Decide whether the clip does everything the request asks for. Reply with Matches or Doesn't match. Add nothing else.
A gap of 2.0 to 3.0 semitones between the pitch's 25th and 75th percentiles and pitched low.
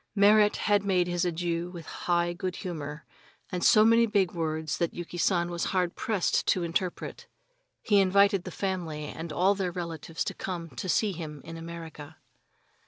Doesn't match